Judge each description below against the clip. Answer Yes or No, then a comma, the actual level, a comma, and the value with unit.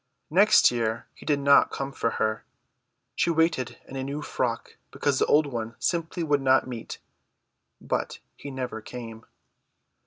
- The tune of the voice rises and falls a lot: No, average, 4.0 semitones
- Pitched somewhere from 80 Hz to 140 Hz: Yes, low, 135 Hz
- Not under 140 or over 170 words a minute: Yes, average, 155 wpm